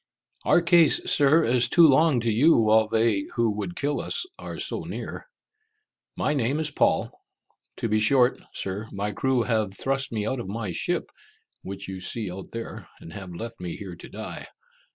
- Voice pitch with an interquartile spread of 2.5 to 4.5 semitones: No, average, 5.0 semitones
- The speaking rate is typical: Yes, average, 185 wpm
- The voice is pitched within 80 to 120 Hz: Yes, low, 115 Hz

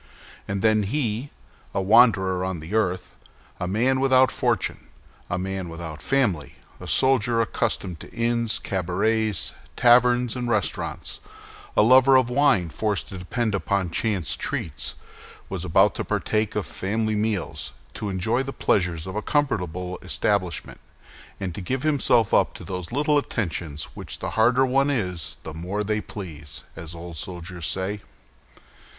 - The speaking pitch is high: No, low, 105 Hz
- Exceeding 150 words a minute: No, average, 145 wpm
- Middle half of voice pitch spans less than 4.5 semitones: No, average, 4.9 semitones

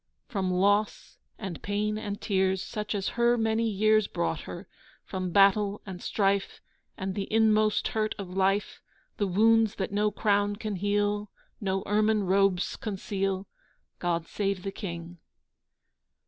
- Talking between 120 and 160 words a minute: Yes, average, 140 wpm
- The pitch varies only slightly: Yes, narrow, 1.9 semitones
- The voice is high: Yes, high, 200 Hz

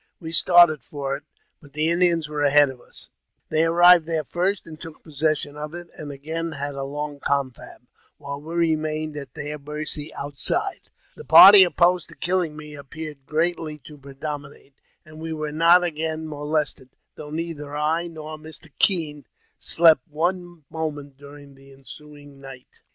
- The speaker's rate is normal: Yes, average, 160 wpm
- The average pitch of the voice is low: No, medium, 155 Hz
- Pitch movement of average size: No, narrow, 2.2 semitones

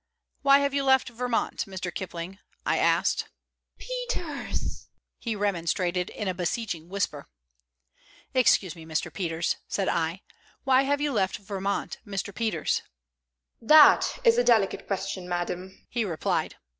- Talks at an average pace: No, slow, 130 wpm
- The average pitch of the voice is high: Yes, high, 195 Hz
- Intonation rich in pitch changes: Yes, wide, 6.3 semitones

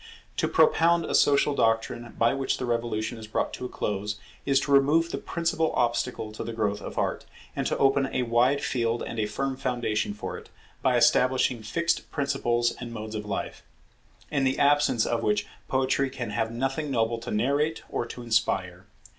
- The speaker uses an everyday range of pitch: Yes, average, 3.5 semitones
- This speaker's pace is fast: No, average, 190 wpm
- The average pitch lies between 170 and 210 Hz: No, low, 120 Hz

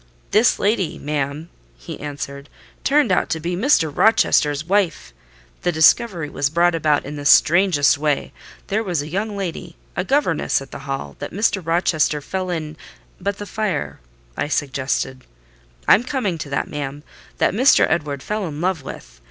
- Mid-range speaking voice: Yes, medium, 160 Hz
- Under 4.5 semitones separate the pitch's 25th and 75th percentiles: No, average, 5.1 semitones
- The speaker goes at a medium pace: Yes, average, 160 wpm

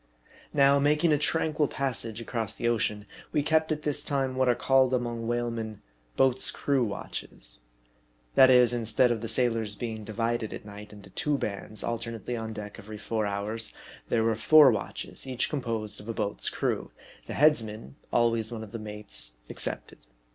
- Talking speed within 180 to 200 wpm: Yes, average, 185 wpm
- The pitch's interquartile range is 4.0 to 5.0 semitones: No, average, 3.5 semitones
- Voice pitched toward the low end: Yes, low, 115 Hz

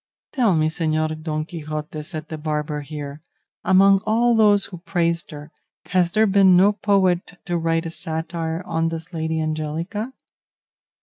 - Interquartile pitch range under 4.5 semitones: Yes, average, 3.2 semitones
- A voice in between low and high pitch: Yes, medium, 165 Hz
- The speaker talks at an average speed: Yes, average, 150 wpm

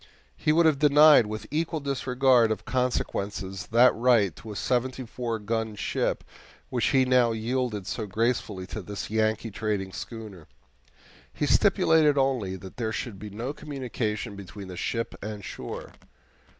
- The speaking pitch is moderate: No, low, 115 Hz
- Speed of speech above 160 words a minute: No, average, 150 wpm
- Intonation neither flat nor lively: Yes, average, 3.6 semitones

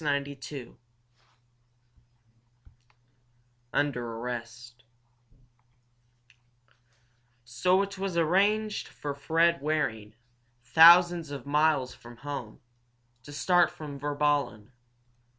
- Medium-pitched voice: Yes, medium, 145 Hz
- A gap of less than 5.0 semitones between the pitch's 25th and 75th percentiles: No, wide, 5.4 semitones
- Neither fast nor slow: No, slow, 80 wpm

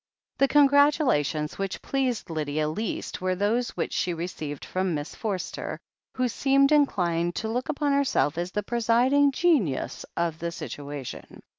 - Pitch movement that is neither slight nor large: No, wide, 8.7 semitones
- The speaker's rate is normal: Yes, average, 145 wpm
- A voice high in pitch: Yes, high, 200 Hz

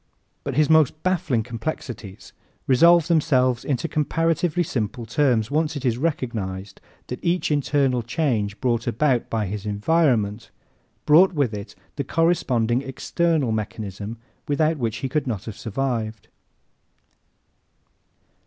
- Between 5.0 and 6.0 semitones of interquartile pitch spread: Yes, wide, 5.6 semitones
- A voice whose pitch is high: No, low, 130 Hz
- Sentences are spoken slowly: Yes, slow, 125 wpm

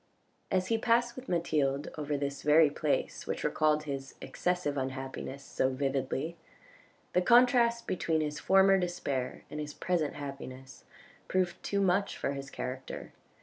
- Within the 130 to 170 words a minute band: Yes, average, 145 wpm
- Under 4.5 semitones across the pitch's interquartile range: No, average, 5.0 semitones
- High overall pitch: No, medium, 150 Hz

